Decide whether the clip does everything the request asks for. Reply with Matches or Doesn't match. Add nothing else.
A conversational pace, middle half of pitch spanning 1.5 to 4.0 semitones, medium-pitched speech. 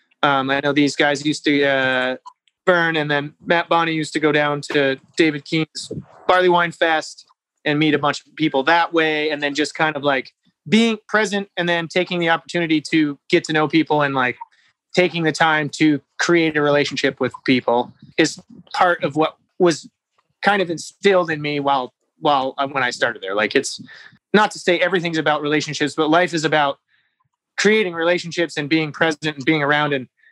Matches